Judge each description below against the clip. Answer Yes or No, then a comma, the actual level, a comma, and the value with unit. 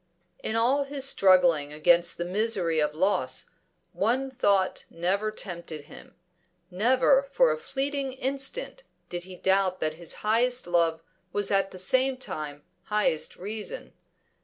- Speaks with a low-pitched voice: No, high, 200 Hz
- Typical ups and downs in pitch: No, wide, 6.9 semitones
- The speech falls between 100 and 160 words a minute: Yes, slow, 135 wpm